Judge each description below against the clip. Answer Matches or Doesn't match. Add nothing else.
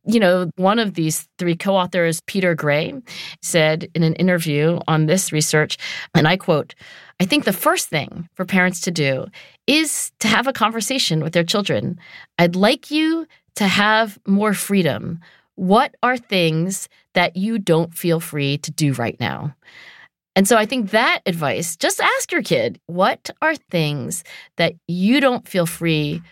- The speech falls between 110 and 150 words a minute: Doesn't match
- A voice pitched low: Doesn't match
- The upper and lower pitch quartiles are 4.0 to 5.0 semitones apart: Matches